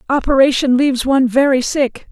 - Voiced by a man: No, female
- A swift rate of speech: No, average, 140 wpm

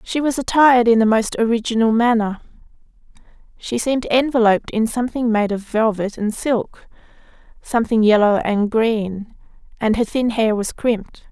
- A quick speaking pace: No, average, 150 wpm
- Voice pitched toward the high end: Yes, high, 225 Hz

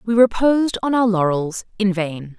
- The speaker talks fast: No, average, 150 wpm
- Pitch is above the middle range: Yes, high, 205 Hz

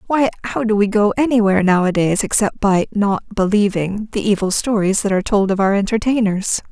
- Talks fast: No, average, 180 wpm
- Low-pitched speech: No, high, 205 Hz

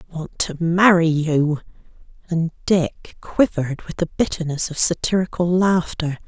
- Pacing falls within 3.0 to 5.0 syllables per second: Yes, 4.3 syllables/s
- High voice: No, medium, 165 Hz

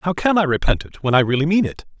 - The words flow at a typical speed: No, fast, 300 wpm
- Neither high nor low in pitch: Yes, medium, 155 Hz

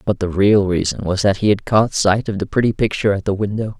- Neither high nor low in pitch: No, low, 100 Hz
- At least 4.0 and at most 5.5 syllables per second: No, 6.0 syllables/s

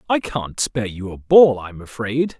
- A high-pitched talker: No, low, 120 Hz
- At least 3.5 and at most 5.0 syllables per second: Yes, 4.6 syllables/s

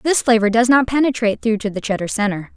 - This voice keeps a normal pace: No, fast, 235 wpm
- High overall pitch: Yes, high, 230 Hz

